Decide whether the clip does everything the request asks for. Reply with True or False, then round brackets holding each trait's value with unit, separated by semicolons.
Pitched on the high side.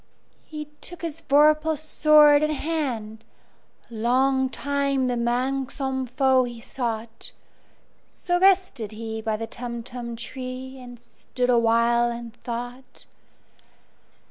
True (255 Hz)